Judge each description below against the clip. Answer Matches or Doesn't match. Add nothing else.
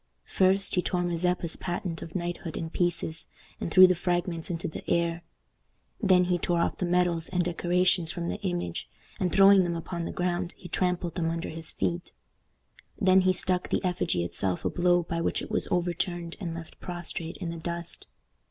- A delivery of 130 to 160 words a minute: Doesn't match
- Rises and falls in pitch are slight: Matches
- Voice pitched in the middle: Matches